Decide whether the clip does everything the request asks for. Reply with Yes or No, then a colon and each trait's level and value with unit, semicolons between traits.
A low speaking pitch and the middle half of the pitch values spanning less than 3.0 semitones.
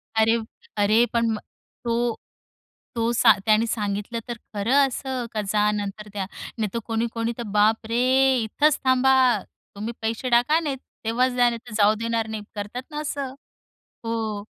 No: high, 230 Hz; narrow, 2.4 semitones